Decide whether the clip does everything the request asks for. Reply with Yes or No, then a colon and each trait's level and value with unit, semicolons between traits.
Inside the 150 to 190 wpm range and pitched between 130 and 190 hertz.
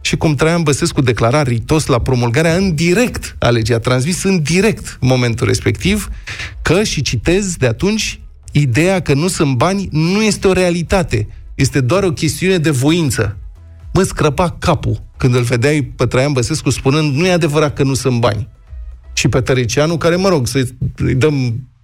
Yes: fast, 170 wpm; medium, 140 Hz